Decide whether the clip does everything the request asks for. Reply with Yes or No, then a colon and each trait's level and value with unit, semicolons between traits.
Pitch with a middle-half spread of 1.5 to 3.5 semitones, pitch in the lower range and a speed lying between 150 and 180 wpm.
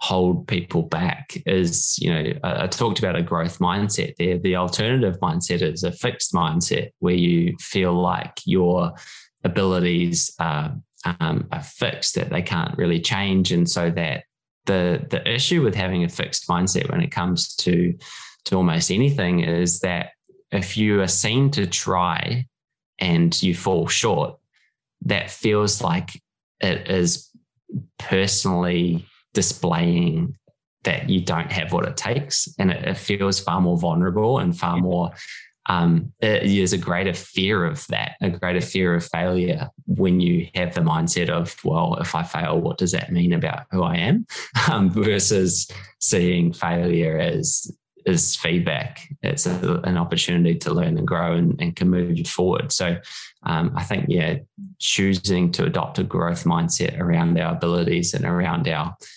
Yes: narrow, 2.4 semitones; very low, 90 Hz; average, 160 wpm